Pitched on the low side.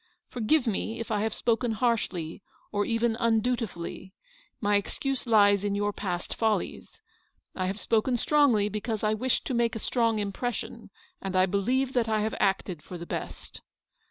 No: high, 220 Hz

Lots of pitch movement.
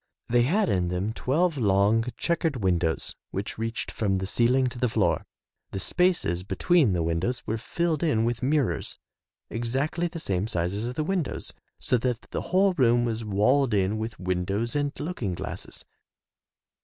Yes: wide, 6.4 semitones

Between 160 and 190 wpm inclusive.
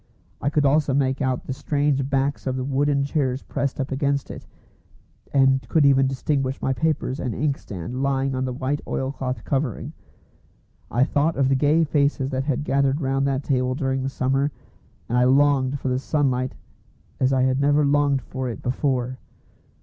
Yes: average, 180 wpm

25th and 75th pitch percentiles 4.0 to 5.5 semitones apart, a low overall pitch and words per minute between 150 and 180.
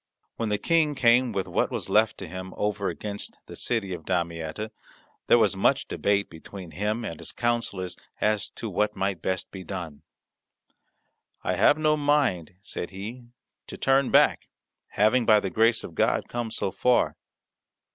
Yes: average, 4.3 semitones; low, 105 Hz; average, 165 wpm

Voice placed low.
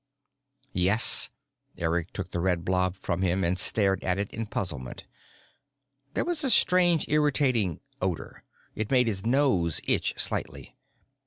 Yes: very low, 95 Hz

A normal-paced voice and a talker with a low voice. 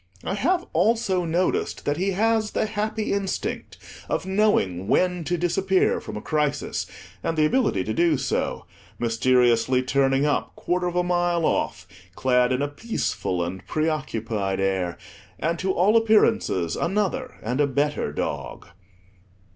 No: average, 150 wpm; medium, 160 Hz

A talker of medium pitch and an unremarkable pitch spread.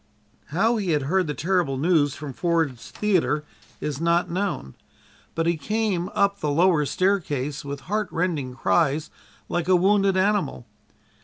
Yes: medium, 170 Hz; average, 4.4 semitones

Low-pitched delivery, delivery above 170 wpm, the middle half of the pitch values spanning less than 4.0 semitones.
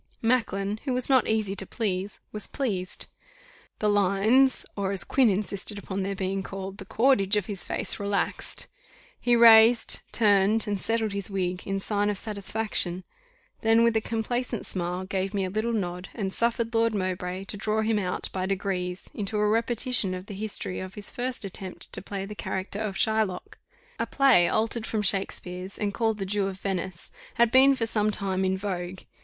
No: high, 205 Hz; average, 185 wpm; average, 2.7 semitones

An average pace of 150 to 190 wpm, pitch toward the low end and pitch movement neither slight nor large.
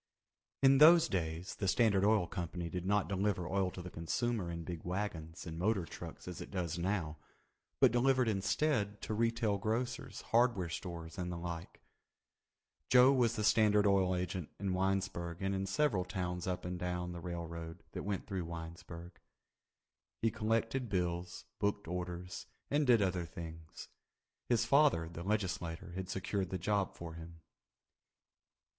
Yes: average, 155 wpm; very low, 95 Hz; average, 3.5 semitones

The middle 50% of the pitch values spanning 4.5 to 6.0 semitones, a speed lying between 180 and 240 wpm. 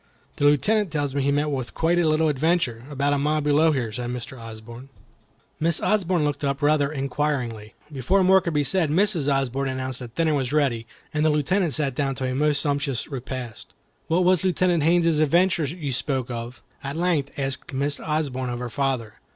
No: average, 3.4 semitones; average, 190 wpm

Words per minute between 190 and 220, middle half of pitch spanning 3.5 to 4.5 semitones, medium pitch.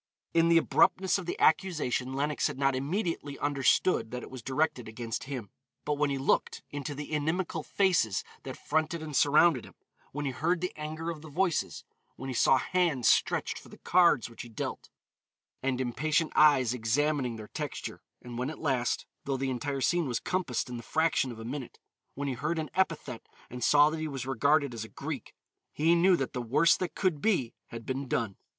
Yes: average, 200 wpm; average, 4.2 semitones; medium, 145 Hz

